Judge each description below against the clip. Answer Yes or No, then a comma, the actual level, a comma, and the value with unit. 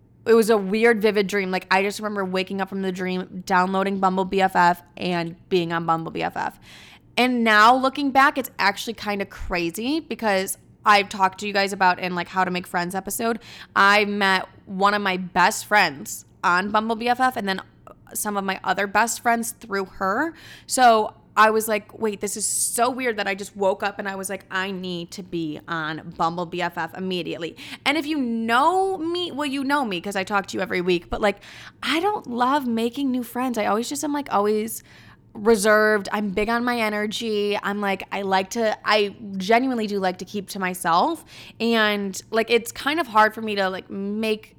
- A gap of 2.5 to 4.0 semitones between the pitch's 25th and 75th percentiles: Yes, average, 3.4 semitones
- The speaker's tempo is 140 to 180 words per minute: No, fast, 205 wpm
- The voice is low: No, high, 205 Hz